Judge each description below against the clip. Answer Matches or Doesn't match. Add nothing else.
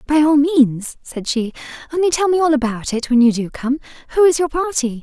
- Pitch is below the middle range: Doesn't match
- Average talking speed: Doesn't match